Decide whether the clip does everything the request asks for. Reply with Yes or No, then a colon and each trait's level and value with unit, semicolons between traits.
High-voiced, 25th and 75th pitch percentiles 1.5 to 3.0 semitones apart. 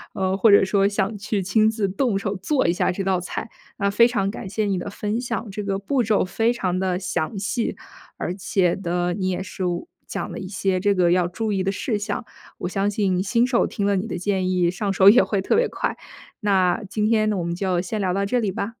Yes: high, 195 Hz; narrow, 2.5 semitones